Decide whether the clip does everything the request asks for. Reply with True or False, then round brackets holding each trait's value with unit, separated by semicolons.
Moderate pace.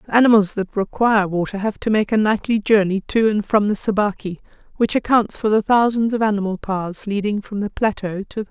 False (220 wpm)